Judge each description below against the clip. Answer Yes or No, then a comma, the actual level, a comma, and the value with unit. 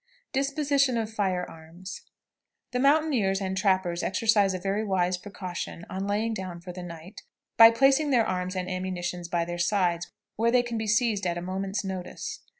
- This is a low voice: No, high, 195 Hz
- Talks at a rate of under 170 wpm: No, average, 175 wpm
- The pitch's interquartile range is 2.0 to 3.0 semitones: No, average, 4.0 semitones